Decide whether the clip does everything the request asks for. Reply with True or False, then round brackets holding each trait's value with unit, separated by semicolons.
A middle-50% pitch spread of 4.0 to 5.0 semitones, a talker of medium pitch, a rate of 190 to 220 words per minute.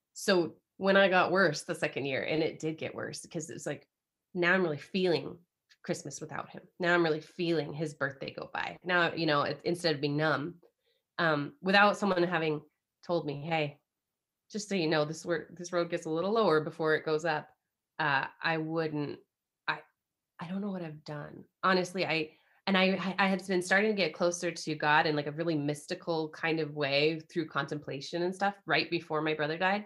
False (2.8 semitones; 165 Hz; 205 wpm)